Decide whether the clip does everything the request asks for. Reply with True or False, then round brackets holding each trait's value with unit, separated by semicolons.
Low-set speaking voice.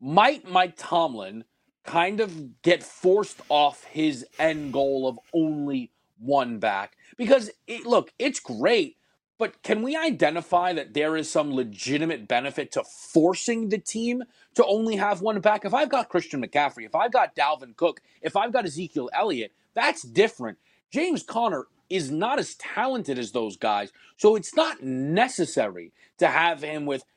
False (170 Hz)